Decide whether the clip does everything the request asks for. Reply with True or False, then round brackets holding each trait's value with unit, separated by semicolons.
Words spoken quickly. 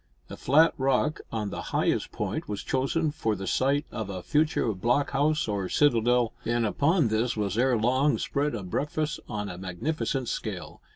False (175 wpm)